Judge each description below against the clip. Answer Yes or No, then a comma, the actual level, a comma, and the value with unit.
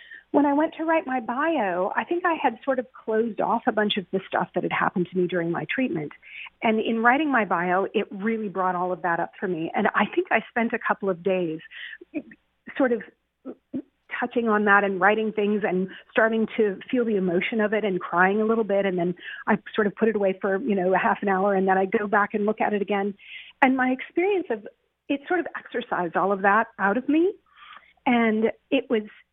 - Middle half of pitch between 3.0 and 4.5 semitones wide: No, average, 5.0 semitones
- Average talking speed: No, fast, 235 wpm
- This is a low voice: No, high, 220 Hz